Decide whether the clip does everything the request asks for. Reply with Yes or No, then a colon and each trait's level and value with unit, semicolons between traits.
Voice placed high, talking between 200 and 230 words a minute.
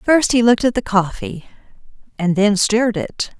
No: high, 215 Hz; average, 175 wpm